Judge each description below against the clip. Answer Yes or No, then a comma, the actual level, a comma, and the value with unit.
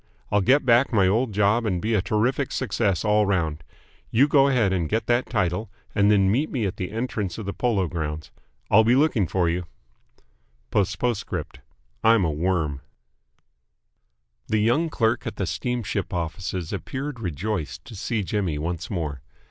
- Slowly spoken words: No, average, 165 wpm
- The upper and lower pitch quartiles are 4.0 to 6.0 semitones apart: Yes, average, 4.8 semitones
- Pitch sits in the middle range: No, low, 105 Hz